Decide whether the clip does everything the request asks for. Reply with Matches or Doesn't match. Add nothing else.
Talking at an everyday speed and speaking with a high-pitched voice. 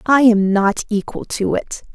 Matches